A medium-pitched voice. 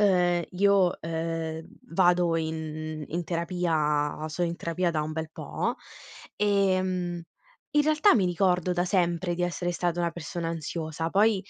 Yes: medium, 175 Hz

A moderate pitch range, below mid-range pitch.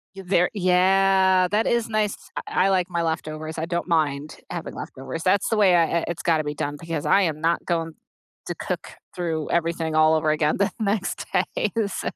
No: average, 3.2 semitones; medium, 170 Hz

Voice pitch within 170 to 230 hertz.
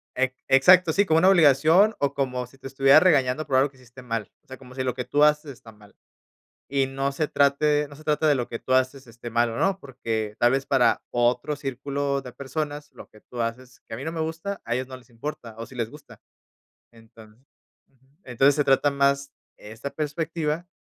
No: low, 135 Hz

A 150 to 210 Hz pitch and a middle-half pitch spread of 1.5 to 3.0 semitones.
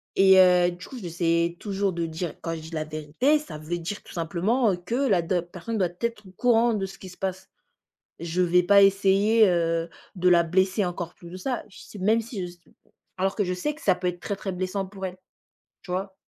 Yes: medium, 185 Hz; average, 2.7 semitones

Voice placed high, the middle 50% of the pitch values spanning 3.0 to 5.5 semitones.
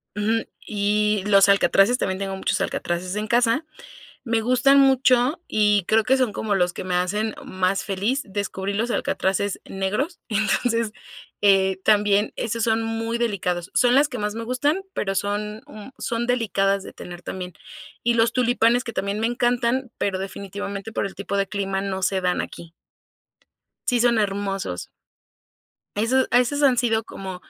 Yes: high, 210 Hz; average, 3.4 semitones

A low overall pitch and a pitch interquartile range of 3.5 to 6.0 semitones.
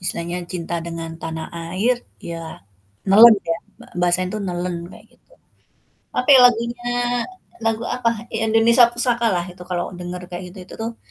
No: medium, 185 Hz; average, 5.1 semitones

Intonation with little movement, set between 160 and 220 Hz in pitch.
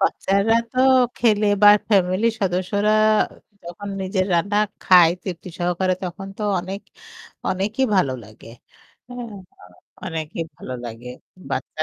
No: average, 3.0 semitones; high, 190 Hz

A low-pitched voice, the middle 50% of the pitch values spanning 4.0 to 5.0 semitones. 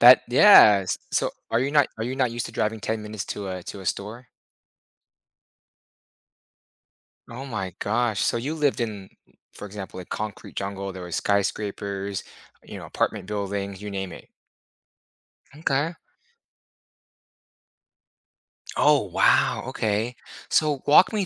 Yes: low, 105 Hz; average, 4.3 semitones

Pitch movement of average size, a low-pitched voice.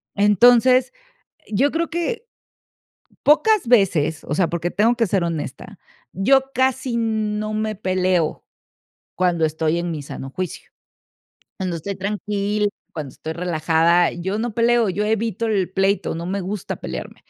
No: average, 5.0 semitones; high, 200 Hz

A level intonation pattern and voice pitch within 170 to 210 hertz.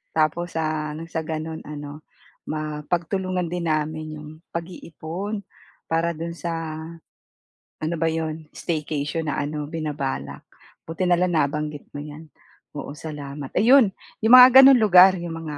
No: narrow, 2.2 semitones; medium, 160 Hz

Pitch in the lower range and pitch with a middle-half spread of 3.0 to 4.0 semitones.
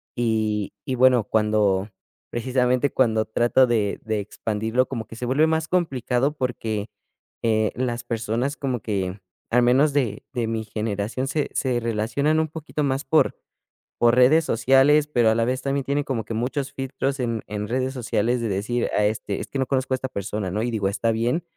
Yes: low, 120 Hz; average, 3.3 semitones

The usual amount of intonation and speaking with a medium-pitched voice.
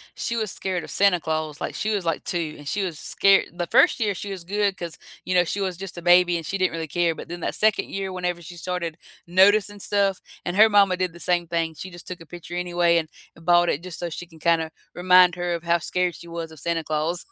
No: narrow, 1.9 semitones; medium, 175 Hz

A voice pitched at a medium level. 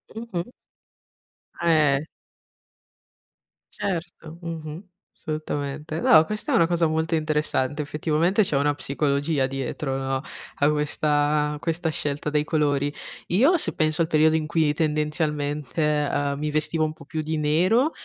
Yes: medium, 155 Hz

